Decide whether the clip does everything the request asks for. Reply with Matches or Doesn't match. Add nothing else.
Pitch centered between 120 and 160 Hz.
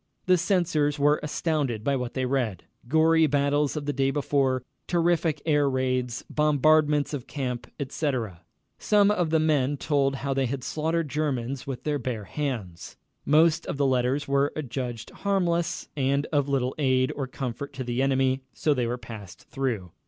Matches